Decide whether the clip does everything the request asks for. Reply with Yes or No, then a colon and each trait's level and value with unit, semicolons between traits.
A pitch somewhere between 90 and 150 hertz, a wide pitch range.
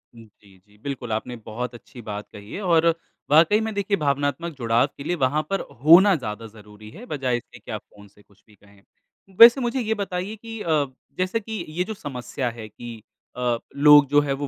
Yes: medium, 140 Hz; wide, 8.2 semitones